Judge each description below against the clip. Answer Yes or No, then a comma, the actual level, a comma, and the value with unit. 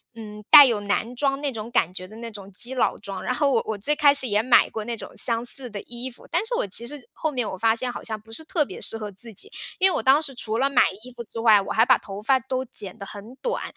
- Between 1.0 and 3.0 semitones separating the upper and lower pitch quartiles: No, average, 4.0 semitones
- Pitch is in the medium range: No, high, 235 Hz